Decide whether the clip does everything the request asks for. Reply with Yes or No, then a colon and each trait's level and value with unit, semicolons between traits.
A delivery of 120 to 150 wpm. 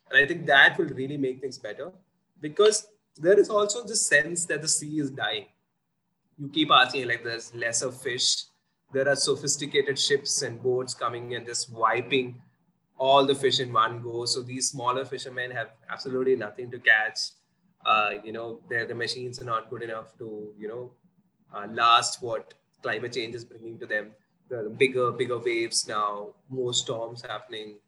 No: average, 175 wpm